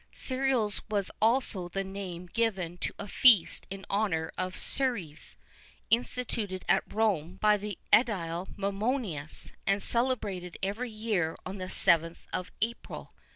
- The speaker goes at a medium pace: No, slow, 130 wpm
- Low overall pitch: No, high, 200 Hz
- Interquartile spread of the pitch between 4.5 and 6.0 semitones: No, average, 3.9 semitones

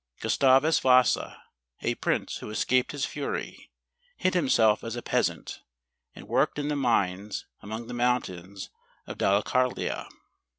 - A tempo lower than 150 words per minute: Yes, average, 140 wpm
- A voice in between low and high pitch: No, low, 125 Hz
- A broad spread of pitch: No, average, 4.1 semitones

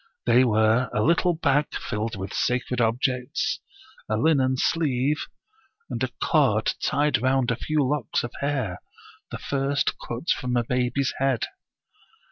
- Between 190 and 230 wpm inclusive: No, average, 140 wpm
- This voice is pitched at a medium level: No, low, 130 Hz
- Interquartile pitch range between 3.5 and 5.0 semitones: No, average, 3.1 semitones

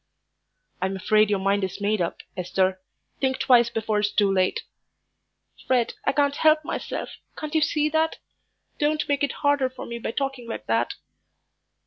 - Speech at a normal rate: Yes, average, 165 wpm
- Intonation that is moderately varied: No, wide, 6.4 semitones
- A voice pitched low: No, high, 235 Hz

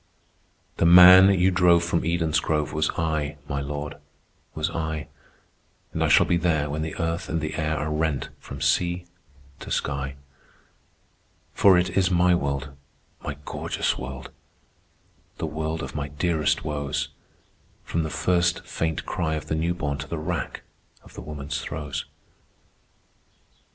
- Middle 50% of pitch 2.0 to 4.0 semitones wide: Yes, average, 2.7 semitones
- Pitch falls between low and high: No, very low, 80 Hz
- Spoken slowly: No, average, 150 wpm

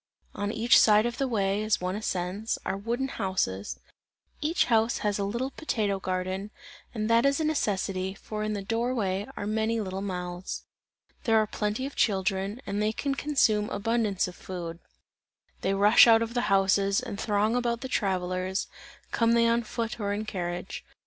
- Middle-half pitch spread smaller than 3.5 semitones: Yes, average, 3.1 semitones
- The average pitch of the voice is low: No, high, 210 Hz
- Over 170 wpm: Yes, average, 180 wpm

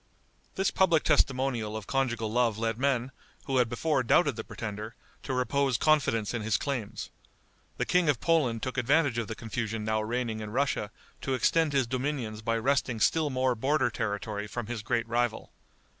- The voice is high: No, low, 120 Hz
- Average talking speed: Yes, average, 175 wpm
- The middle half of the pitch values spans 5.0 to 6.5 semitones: No, average, 3.6 semitones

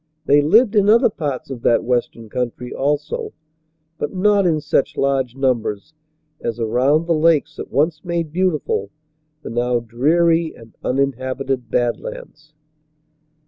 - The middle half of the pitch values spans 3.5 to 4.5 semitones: No, average, 5.2 semitones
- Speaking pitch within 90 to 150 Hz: Yes, medium, 140 Hz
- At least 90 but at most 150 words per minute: Yes, average, 140 wpm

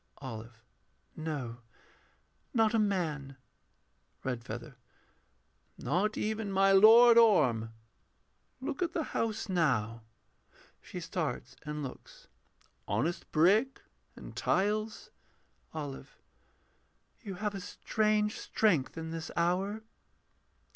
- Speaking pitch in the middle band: Yes, medium, 180 Hz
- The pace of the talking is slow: Yes, slow, 95 wpm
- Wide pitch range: Yes, wide, 7.7 semitones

